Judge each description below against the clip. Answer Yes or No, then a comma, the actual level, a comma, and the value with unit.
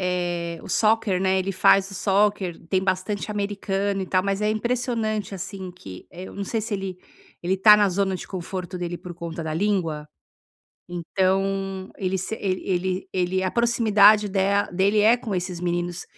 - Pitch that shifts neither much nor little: No, narrow, 2.1 semitones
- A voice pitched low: No, high, 190 Hz